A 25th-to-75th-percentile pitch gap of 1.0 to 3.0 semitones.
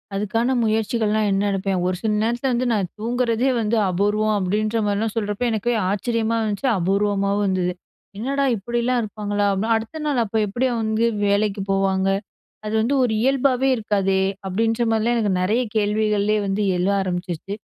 Yes: average, 2.7 semitones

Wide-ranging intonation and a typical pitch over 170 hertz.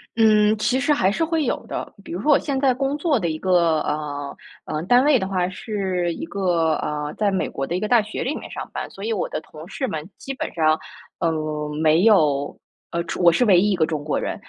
Yes: wide, 6.5 semitones; high, 190 Hz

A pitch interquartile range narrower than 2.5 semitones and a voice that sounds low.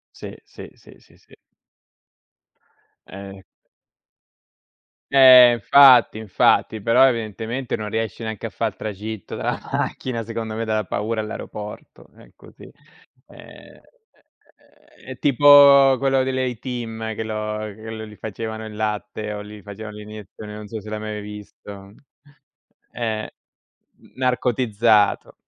Yes: narrow, 2.1 semitones; low, 110 Hz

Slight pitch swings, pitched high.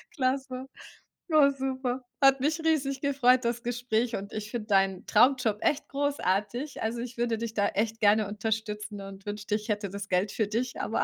No: average, 3.9 semitones; high, 230 Hz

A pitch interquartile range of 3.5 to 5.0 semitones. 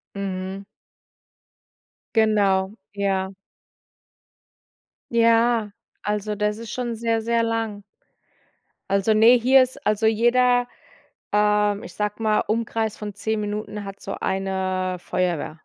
No: narrow, 2.5 semitones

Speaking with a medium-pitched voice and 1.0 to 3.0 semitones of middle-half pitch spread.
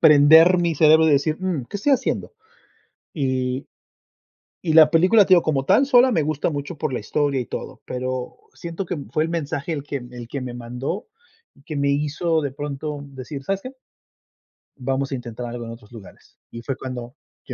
No: medium, 145 Hz; average, 4.2 semitones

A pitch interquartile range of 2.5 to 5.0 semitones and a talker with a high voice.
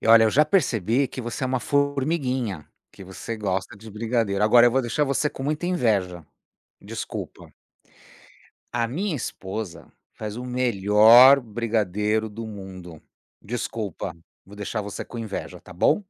No: average, 4.0 semitones; low, 115 Hz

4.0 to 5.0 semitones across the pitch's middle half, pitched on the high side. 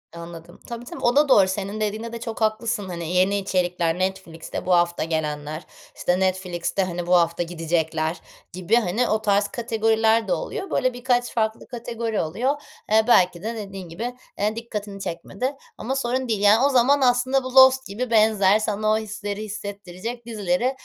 Yes: average, 4.6 semitones; high, 210 Hz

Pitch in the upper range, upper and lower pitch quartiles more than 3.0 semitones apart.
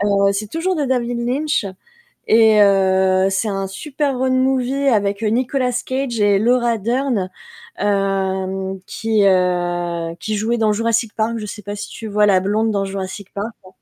Yes: high, 210 Hz; average, 3.6 semitones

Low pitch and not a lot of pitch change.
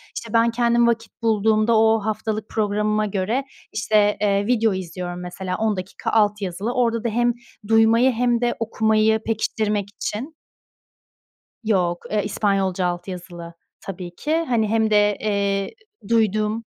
No: high, 215 Hz; narrow, 2.3 semitones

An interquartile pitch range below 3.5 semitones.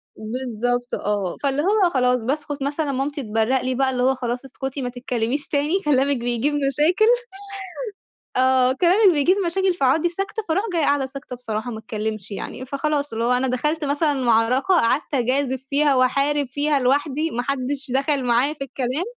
Yes: average, 2.9 semitones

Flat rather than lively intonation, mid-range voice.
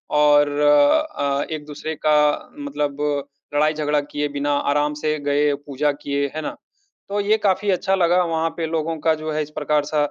Yes: narrow, 1.7 semitones; medium, 150 Hz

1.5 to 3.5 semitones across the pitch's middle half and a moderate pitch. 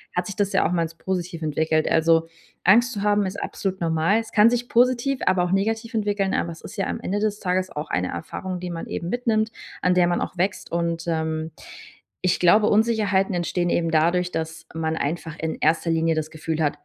No: average, 3.9 semitones; medium, 180 Hz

